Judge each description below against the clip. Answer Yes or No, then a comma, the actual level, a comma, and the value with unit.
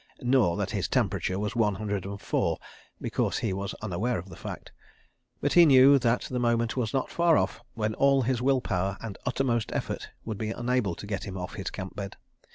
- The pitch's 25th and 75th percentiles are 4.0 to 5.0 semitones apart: Yes, average, 4.3 semitones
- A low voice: Yes, low, 110 Hz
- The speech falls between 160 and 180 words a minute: No, fast, 205 wpm